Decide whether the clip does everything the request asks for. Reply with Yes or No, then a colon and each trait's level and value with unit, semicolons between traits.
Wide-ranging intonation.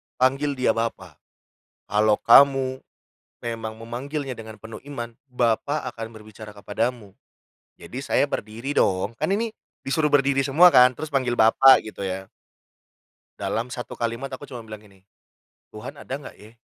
No: average, 3.8 semitones